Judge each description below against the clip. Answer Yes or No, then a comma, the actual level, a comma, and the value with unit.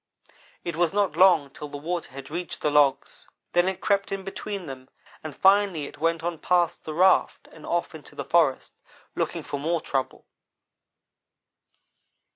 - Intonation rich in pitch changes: No, average, 3.8 semitones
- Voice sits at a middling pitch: Yes, medium, 165 Hz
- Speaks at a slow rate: No, average, 165 wpm